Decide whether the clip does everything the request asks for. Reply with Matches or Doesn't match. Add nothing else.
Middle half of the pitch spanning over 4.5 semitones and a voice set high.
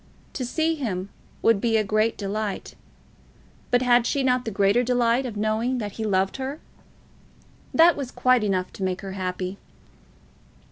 Doesn't match